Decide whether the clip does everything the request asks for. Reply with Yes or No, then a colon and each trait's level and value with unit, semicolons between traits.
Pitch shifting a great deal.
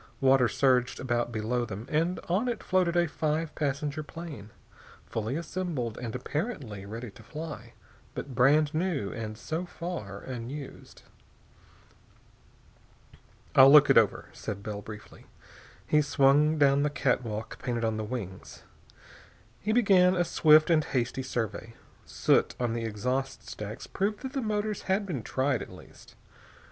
Yes: wide, 6.0 semitones